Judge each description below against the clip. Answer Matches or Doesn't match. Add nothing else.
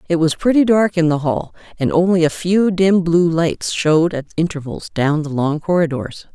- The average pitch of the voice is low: Doesn't match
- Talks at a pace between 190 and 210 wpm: Matches